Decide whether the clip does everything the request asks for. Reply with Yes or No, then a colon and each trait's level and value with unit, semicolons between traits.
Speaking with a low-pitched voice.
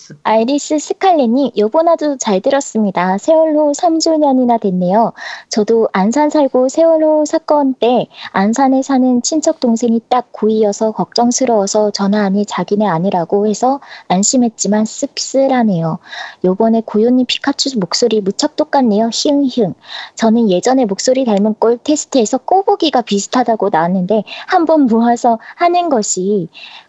No: high, 240 Hz